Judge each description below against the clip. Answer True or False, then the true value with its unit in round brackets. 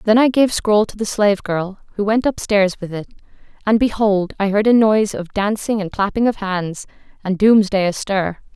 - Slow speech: False (195 wpm)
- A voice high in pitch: True (205 Hz)